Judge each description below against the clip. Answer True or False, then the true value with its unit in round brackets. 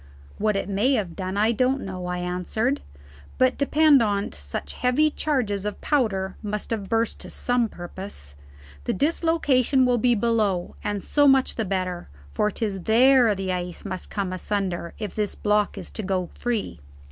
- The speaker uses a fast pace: False (170 wpm)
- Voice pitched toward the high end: True (210 Hz)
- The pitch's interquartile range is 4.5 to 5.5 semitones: True (4.8 semitones)